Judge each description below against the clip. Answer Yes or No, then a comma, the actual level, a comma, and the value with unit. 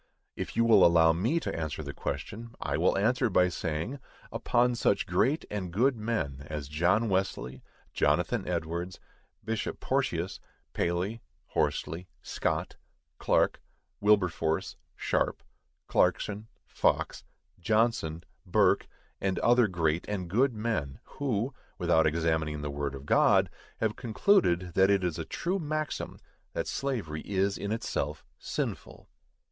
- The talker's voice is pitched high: No, very low, 95 Hz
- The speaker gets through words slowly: Yes, slow, 130 wpm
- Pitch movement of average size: No, wide, 5.9 semitones